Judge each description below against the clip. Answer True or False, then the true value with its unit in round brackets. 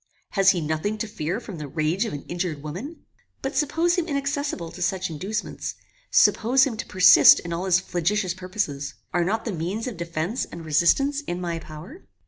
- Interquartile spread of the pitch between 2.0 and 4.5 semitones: False (5.3 semitones)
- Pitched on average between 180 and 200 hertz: True (185 Hz)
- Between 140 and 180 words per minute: False (190 wpm)